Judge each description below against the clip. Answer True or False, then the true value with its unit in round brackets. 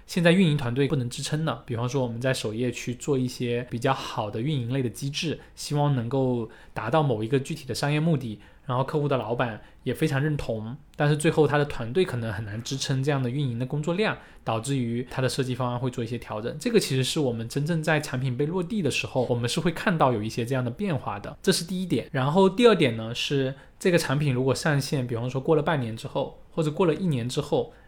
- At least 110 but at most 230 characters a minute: False (365 characters per minute)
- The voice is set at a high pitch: False (135 Hz)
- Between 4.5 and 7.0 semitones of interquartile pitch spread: False (3.9 semitones)